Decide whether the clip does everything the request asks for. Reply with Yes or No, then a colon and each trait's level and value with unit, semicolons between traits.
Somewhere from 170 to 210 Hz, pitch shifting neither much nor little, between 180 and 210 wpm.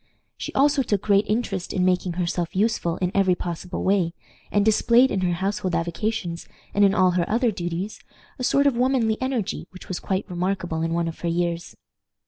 Yes: high, 190 Hz; average, 3.9 semitones; average, 190 wpm